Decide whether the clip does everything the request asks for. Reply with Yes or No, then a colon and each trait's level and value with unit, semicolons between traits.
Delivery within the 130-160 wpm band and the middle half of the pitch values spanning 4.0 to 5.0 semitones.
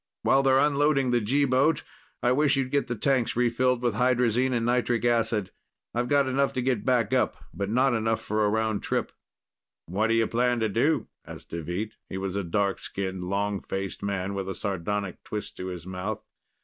No: average, 200 wpm; average, 4.3 semitones